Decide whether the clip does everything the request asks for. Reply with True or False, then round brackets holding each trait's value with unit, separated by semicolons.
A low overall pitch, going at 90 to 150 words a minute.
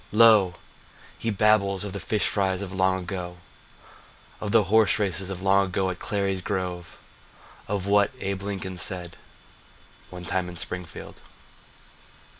True (95 Hz; 140 wpm)